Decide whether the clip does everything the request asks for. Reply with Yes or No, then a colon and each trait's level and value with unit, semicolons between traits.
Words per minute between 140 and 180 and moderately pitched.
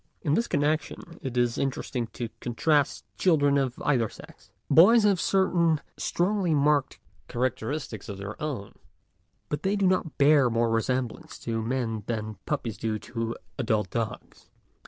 No: average, 150 wpm; low, 130 Hz